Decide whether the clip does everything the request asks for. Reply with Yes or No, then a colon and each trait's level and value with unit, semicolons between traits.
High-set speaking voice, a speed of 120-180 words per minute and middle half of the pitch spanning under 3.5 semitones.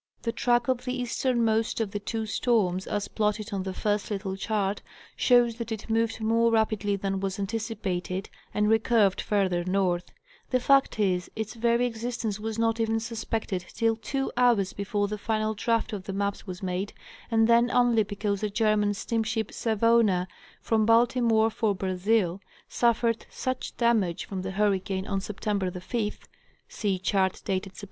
Yes: high, 215 Hz; average, 170 wpm; average, 2.7 semitones